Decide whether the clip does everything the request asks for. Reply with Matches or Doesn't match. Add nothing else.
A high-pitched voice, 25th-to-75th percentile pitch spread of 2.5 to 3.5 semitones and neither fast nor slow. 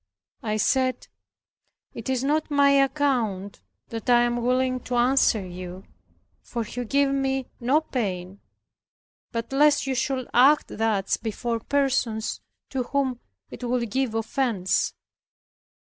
Doesn't match